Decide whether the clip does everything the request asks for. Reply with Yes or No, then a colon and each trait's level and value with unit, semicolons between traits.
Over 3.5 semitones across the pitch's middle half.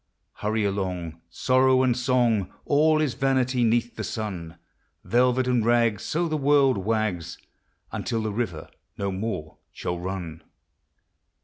Yes: average, 5.2 semitones